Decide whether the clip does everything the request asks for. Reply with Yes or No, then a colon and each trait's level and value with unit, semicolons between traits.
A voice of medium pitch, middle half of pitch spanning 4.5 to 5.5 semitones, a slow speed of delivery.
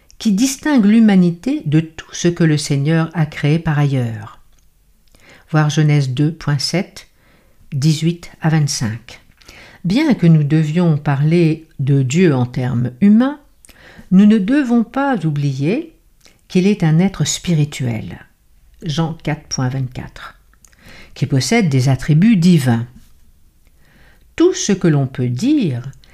Yes: medium, 155 Hz; average, 5.2 semitones; slow, 120 wpm